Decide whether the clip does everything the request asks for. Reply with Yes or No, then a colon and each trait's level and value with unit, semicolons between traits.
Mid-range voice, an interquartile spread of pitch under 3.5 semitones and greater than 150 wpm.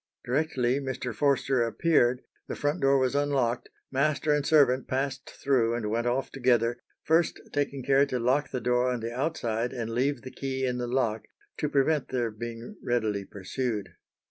No: low, 130 Hz; average, 2.8 semitones; average, 170 wpm